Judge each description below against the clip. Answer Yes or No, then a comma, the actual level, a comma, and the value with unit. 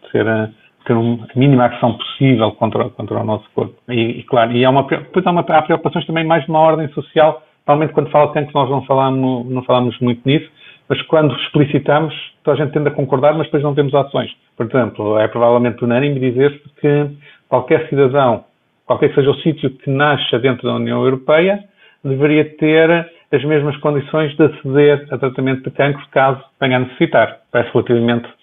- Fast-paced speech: Yes, fast, 190 wpm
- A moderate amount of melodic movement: Yes, average, 3.7 semitones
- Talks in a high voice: No, medium, 140 Hz